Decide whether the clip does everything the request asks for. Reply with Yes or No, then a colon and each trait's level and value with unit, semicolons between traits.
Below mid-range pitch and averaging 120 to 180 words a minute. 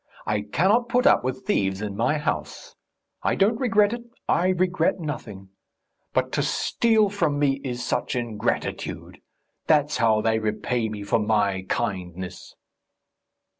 Yes: low, 125 Hz; average, 140 wpm